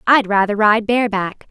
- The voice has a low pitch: No, high, 215 Hz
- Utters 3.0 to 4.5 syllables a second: No, 5.2 syllables/s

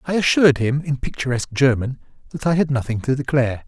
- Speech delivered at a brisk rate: No, average, 195 wpm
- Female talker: No, male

